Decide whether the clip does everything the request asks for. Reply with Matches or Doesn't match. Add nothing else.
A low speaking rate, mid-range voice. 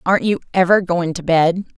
Doesn't match